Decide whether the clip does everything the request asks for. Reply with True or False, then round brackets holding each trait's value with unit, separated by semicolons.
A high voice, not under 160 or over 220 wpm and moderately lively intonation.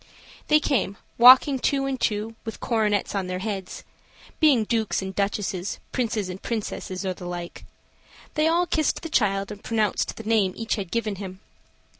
True (215 Hz; 175 wpm; 4.0 semitones)